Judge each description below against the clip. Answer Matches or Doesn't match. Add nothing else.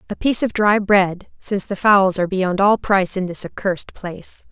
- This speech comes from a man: Doesn't match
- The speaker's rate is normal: Doesn't match